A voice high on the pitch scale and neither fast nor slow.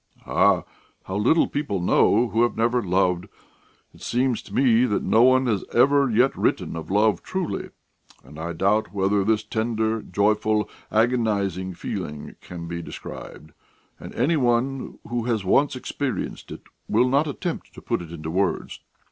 No: low, 110 Hz; average, 160 wpm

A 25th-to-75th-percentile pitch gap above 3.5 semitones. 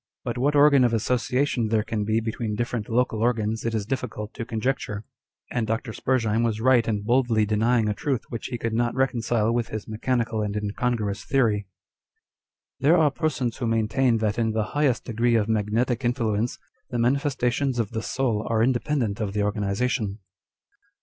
No: narrow, 2.6 semitones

